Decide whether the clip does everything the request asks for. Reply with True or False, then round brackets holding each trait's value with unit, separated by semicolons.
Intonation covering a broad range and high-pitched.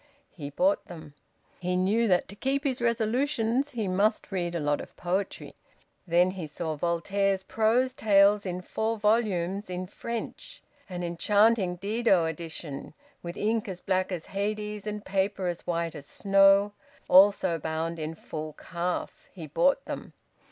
False (3.7 semitones; 195 Hz)